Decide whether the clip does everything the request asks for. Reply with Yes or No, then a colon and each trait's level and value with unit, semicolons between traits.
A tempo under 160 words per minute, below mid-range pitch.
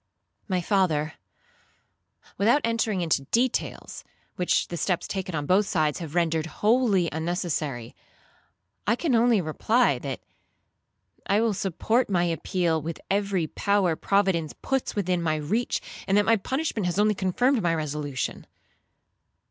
No: slow, 135 wpm; medium, 185 Hz